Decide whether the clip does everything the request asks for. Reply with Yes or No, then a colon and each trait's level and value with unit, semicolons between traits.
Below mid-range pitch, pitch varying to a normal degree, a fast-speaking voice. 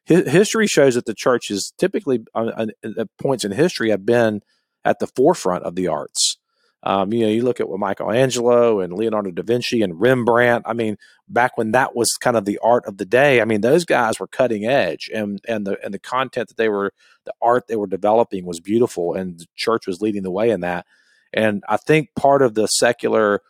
Yes: low, 110 Hz; average, 3.1 semitones; fast, 220 wpm